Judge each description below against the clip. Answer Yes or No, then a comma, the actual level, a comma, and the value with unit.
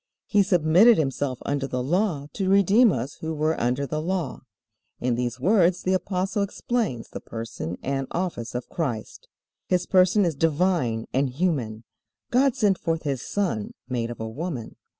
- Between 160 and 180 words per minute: Yes, average, 165 wpm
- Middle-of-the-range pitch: Yes, medium, 160 Hz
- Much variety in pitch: Yes, wide, 6.7 semitones